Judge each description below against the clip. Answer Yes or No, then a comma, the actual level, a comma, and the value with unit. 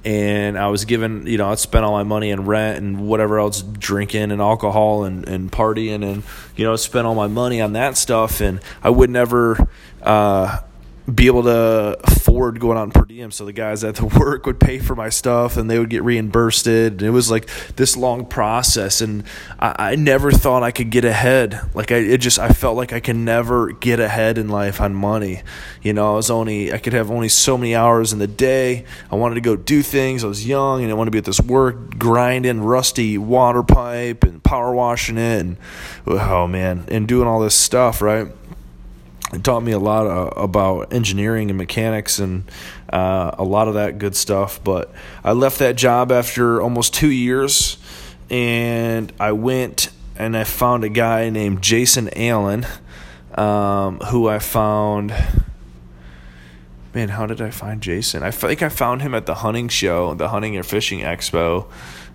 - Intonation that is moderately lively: Yes, average, 3.0 semitones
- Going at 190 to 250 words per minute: Yes, average, 200 wpm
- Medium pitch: No, low, 110 Hz